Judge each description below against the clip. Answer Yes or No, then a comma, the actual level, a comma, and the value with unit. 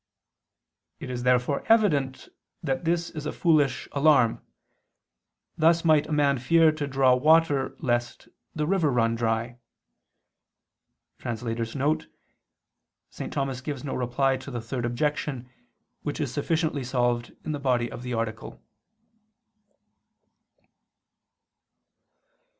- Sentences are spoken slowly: Yes, slow, 110 wpm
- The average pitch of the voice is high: No, low, 135 Hz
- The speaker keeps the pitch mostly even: No, average, 3.8 semitones